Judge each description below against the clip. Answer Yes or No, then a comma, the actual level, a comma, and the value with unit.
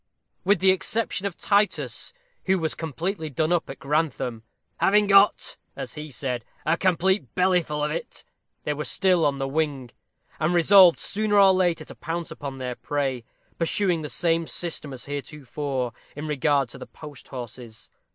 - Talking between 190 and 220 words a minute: No, average, 165 wpm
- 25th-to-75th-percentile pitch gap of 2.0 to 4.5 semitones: No, average, 4.9 semitones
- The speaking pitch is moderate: Yes, medium, 155 Hz